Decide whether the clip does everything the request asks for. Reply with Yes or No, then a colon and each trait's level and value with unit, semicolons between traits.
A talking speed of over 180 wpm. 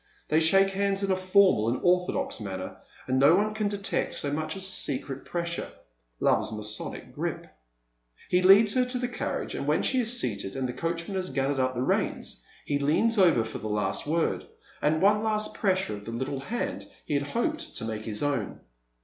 Yes: fast, 205 wpm